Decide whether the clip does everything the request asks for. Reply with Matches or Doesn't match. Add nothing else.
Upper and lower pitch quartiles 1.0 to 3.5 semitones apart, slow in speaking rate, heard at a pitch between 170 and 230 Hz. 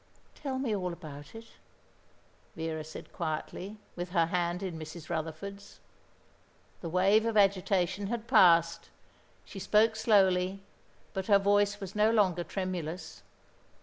Matches